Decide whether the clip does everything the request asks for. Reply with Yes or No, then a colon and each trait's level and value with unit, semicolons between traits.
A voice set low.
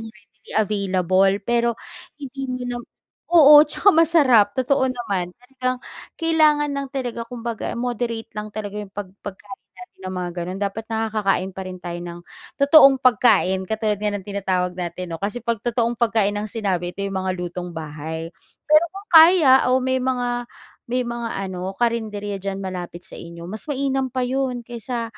No: high, 225 Hz